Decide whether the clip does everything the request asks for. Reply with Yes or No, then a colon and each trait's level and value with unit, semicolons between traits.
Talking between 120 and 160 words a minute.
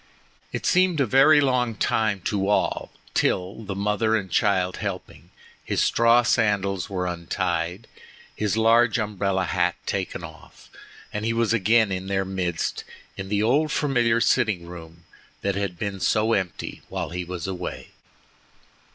Yes: average, 145 wpm